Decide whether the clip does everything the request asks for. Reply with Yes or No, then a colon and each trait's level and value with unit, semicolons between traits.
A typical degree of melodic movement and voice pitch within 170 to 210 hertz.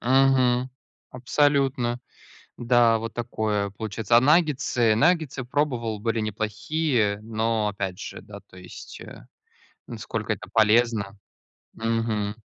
No: average, 3.2 semitones; low, 115 Hz